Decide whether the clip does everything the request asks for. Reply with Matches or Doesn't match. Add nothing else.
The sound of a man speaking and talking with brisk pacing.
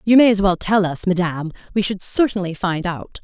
Doesn't match